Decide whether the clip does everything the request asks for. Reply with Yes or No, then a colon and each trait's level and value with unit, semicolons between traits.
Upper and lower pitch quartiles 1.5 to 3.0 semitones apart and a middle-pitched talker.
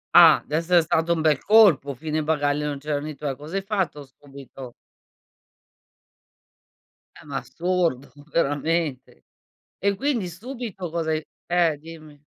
No: average, 3.4 semitones; medium, 155 Hz